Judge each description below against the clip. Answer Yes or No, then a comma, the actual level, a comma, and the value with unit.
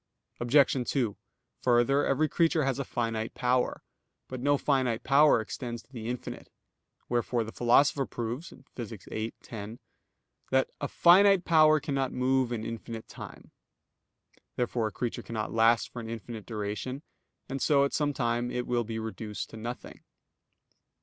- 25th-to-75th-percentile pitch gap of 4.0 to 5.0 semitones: No, average, 3.2 semitones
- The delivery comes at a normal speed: Yes, average, 150 wpm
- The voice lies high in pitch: No, low, 120 Hz